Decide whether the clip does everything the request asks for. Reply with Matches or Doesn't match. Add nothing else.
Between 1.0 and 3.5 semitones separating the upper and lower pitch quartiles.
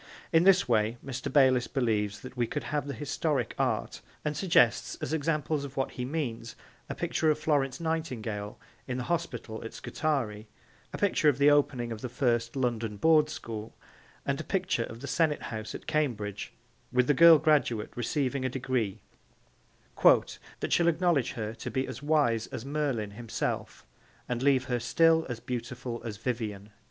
Doesn't match